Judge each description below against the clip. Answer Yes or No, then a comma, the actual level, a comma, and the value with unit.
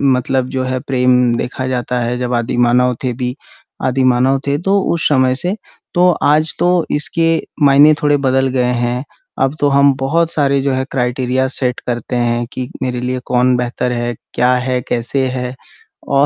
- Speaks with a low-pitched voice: Yes, low, 130 Hz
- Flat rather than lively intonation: Yes, narrow, 1.8 semitones